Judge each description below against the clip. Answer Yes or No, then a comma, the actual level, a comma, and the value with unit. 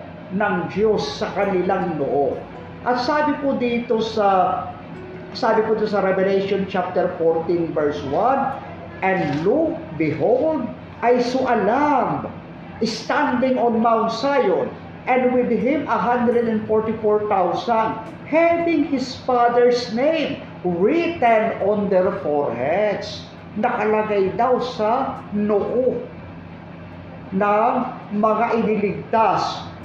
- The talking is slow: Yes, slow, 100 wpm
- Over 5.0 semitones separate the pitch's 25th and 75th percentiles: No, average, 4.1 semitones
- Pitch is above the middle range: Yes, high, 225 Hz